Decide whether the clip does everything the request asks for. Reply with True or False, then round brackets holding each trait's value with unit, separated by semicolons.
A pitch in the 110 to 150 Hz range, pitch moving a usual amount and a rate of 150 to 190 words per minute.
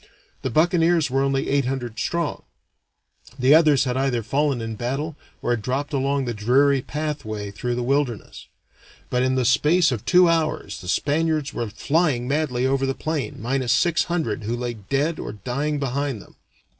True (135 Hz; 3.6 semitones; 175 wpm)